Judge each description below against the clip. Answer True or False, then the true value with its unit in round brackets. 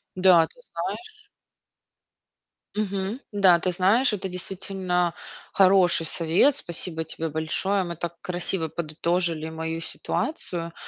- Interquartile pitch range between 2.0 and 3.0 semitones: True (2.7 semitones)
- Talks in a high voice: False (180 Hz)